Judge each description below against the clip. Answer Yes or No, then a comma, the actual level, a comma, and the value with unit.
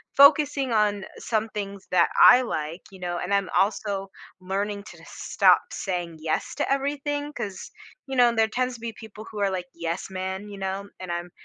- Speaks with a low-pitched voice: No, high, 200 Hz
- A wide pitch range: No, average, 3.9 semitones